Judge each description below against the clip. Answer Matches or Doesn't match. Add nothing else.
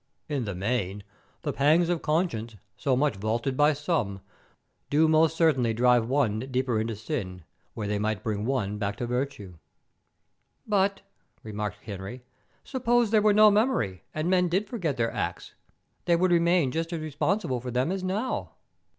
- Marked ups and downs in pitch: Matches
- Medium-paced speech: Matches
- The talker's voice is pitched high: Doesn't match